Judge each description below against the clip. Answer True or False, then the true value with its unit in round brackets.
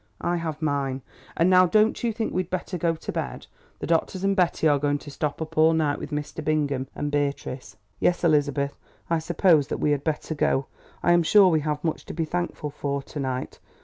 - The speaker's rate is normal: False (220 wpm)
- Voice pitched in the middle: True (155 Hz)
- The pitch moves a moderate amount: True (3.1 semitones)